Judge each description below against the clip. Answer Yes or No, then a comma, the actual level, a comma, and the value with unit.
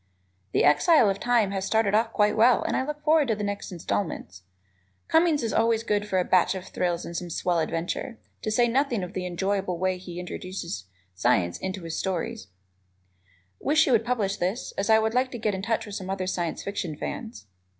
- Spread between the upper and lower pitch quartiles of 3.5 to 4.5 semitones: Yes, average, 4.2 semitones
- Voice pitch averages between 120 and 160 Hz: No, high, 200 Hz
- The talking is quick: Yes, fast, 210 wpm